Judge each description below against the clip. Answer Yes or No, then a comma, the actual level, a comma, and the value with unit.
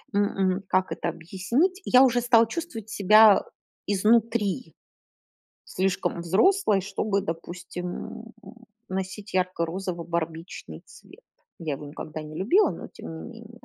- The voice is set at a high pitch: Yes, high, 195 Hz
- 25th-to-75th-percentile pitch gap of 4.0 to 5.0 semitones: Yes, average, 4.4 semitones